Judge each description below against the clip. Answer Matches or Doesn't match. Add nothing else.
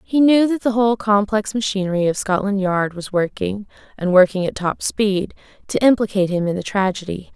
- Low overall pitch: Doesn't match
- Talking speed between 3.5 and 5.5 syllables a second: Matches